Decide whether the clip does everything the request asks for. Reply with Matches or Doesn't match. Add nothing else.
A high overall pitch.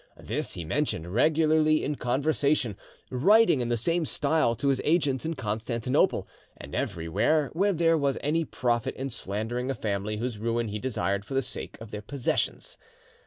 Doesn't match